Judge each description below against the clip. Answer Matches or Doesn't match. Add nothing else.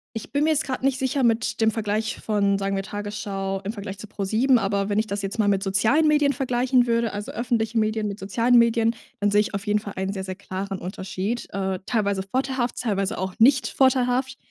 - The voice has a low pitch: Doesn't match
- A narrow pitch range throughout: Doesn't match